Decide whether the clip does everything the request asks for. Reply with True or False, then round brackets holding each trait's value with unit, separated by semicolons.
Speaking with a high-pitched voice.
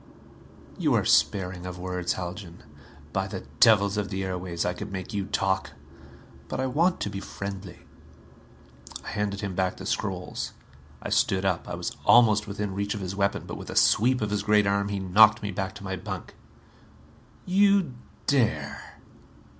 False (100 Hz)